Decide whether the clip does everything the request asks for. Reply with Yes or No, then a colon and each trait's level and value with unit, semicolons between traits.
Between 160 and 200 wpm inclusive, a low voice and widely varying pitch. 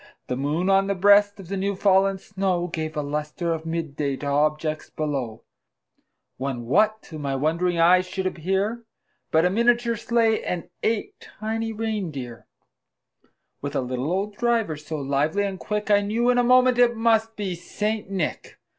No: average, 175 wpm; medium, 185 Hz; wide, 5.8 semitones